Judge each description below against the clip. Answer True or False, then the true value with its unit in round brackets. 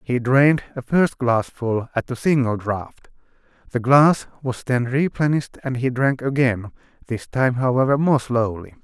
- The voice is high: False (130 Hz)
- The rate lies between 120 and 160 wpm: True (155 wpm)